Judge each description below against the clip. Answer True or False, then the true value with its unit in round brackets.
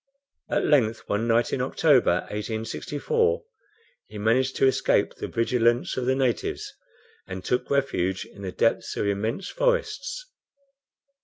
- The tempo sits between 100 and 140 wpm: True (135 wpm)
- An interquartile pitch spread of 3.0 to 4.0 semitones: False (4.4 semitones)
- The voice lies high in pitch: False (120 Hz)